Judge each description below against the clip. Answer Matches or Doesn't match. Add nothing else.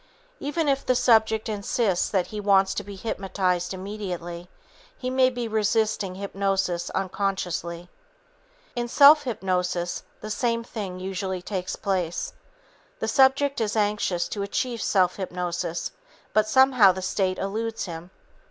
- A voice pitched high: Matches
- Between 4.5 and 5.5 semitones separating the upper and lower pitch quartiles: Doesn't match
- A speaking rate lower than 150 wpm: Matches